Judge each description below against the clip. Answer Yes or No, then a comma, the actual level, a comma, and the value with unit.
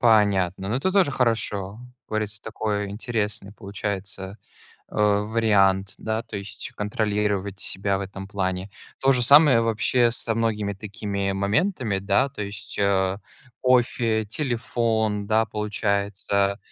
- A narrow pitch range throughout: Yes, narrow, 2.3 semitones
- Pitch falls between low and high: No, low, 105 Hz